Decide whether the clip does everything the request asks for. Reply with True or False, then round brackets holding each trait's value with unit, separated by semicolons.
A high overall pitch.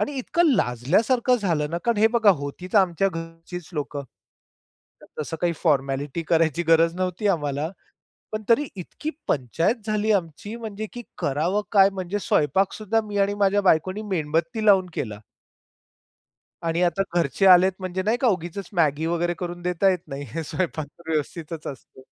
False (175 Hz)